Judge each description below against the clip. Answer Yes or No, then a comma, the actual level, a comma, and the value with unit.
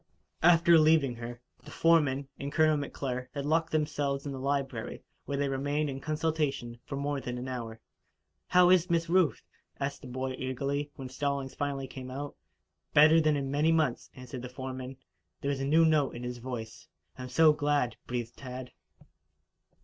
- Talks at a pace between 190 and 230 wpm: No, average, 175 wpm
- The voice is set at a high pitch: No, medium, 140 Hz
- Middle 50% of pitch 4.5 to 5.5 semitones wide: No, average, 3.0 semitones